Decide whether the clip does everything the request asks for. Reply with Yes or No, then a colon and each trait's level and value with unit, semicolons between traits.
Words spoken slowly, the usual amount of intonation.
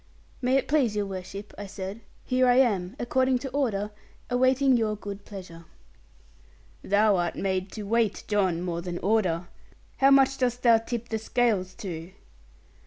No: average, 160 wpm; average, 4.6 semitones